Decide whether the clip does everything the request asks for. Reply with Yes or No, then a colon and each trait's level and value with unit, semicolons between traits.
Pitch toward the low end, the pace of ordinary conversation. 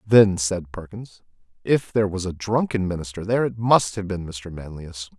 Yes: low, 100 Hz; average, 185 wpm